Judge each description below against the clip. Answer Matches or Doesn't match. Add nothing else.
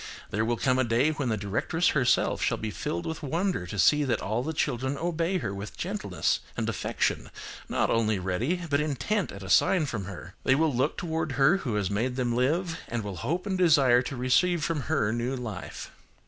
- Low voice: Matches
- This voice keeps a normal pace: Doesn't match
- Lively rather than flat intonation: Matches